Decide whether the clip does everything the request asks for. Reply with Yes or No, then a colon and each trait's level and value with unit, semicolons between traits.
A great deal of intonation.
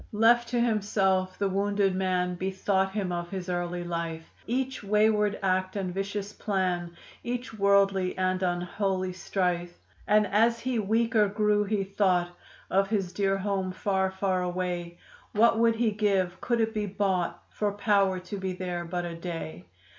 No: narrow, 2.4 semitones